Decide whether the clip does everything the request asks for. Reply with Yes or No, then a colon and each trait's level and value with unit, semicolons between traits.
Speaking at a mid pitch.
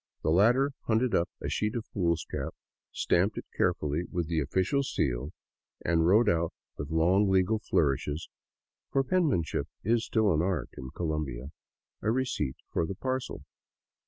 No: very low, 90 Hz